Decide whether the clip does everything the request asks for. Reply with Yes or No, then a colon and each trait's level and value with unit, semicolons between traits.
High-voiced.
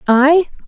Yes: very high, 295 Hz